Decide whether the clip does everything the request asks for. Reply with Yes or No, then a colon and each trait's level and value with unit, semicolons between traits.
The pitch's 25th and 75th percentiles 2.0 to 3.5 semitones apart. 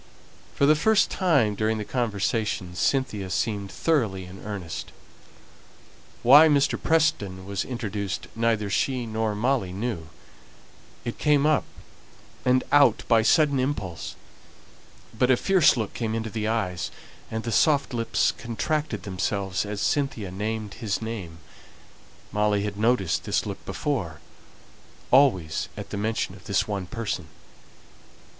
No: average, 4.5 semitones